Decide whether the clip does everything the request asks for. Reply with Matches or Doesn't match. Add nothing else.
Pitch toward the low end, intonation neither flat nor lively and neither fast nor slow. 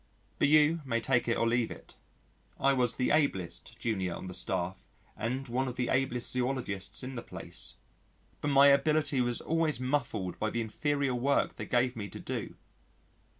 Matches